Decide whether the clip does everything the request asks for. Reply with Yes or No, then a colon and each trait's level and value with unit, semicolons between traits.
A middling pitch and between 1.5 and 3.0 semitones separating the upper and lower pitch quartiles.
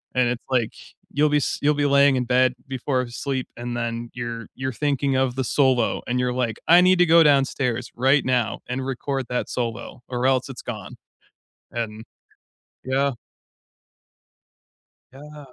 No: low, 130 Hz; narrow, 2.4 semitones